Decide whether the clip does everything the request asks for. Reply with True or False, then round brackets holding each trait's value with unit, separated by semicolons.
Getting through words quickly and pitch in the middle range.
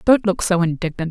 True (215 wpm; 180 Hz)